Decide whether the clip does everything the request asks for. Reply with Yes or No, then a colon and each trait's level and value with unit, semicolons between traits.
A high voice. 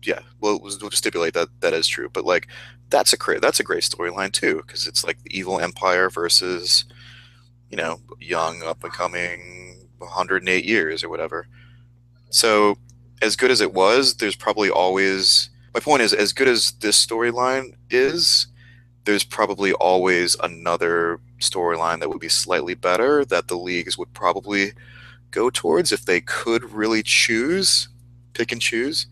No: low, 115 Hz